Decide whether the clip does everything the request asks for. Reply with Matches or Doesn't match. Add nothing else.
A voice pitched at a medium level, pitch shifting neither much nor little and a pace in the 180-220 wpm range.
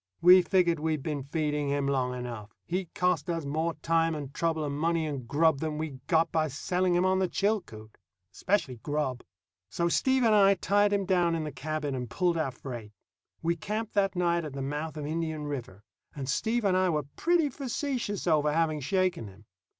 Matches